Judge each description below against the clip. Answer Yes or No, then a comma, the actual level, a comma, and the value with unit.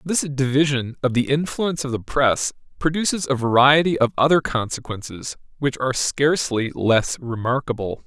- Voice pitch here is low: Yes, low, 130 Hz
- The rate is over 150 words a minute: No, average, 140 wpm